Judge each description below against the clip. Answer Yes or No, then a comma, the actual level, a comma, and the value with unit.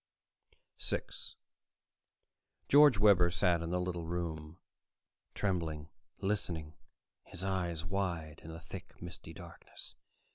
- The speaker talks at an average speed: No, slow, 105 wpm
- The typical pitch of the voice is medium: No, very low, 85 Hz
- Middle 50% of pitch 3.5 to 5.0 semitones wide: No, average, 2.8 semitones